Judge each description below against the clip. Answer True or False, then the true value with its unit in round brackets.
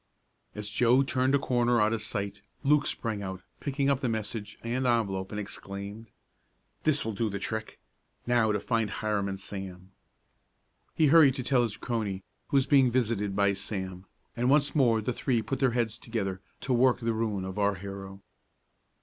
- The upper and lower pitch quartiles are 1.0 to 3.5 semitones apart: False (4.0 semitones)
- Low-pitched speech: True (110 Hz)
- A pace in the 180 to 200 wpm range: True (185 wpm)